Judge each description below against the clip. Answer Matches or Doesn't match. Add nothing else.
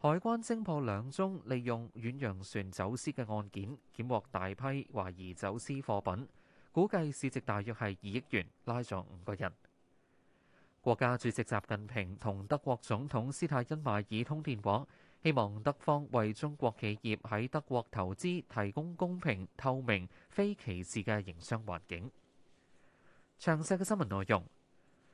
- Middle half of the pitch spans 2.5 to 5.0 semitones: Doesn't match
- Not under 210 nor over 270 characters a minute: Matches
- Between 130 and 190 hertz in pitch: Doesn't match